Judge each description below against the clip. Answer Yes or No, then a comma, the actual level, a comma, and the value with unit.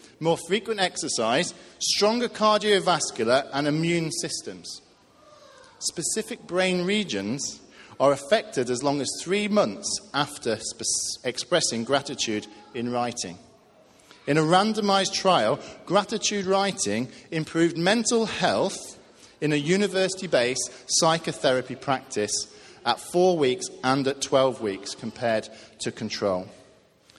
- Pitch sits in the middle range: Yes, medium, 160 Hz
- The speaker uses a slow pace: Yes, slow, 105 wpm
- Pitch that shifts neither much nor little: No, wide, 7.4 semitones